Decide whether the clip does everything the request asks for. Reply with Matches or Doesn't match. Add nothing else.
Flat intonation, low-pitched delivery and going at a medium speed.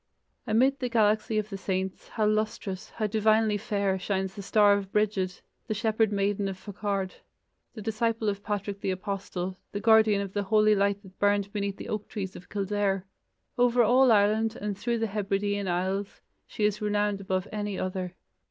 Doesn't match